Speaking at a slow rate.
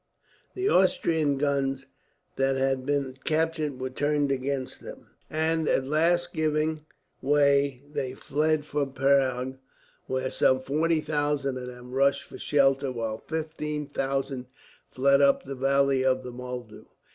Yes: slow, 130 wpm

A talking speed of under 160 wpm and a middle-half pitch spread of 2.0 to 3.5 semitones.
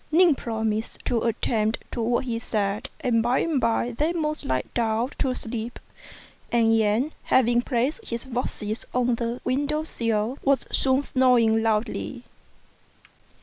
Yes: average, 145 wpm; average, 2.7 semitones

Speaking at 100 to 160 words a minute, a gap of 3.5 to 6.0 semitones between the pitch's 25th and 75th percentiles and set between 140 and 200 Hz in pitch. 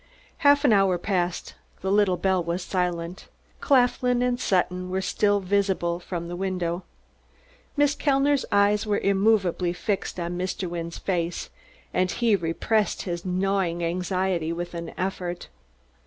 No: average, 140 wpm; average, 2.7 semitones; medium, 185 Hz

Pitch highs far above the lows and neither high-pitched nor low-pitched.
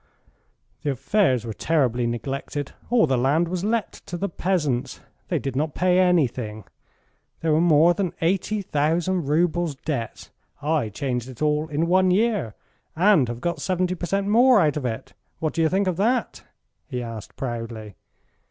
Yes: wide, 5.9 semitones; medium, 160 Hz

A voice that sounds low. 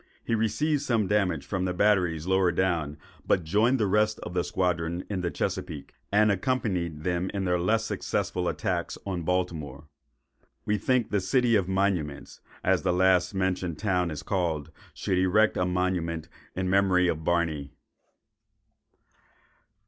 Yes: very low, 90 Hz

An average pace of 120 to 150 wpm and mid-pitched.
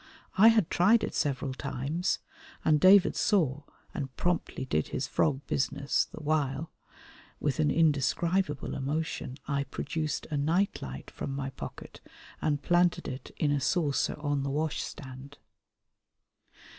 Yes: average, 140 wpm; medium, 145 Hz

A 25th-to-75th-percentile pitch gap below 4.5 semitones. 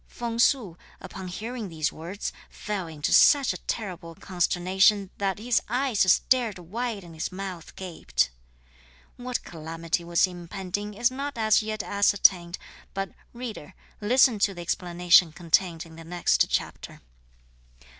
Yes: average, 4.1 semitones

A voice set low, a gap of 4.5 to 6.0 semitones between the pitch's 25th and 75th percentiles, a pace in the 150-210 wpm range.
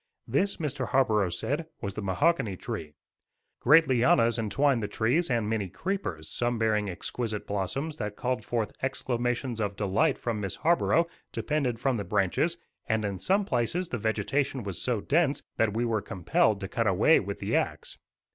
Yes: low, 115 Hz; average, 5.1 semitones; average, 175 wpm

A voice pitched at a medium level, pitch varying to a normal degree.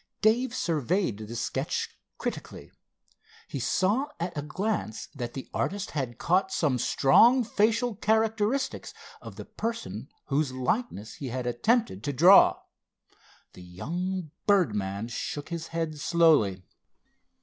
No: medium, 165 Hz; wide, 8.9 semitones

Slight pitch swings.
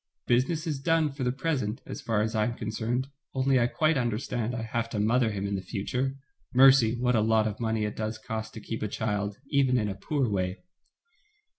No: average, 3.3 semitones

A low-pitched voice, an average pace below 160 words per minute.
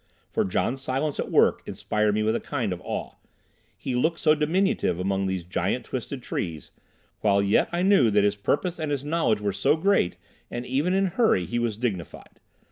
No: low, 120 Hz; average, 195 wpm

